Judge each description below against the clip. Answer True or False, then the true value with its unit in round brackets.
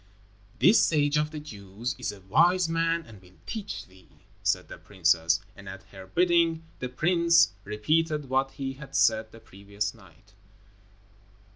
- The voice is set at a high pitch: False (125 Hz)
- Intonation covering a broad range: True (8.8 semitones)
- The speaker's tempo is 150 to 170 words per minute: True (155 wpm)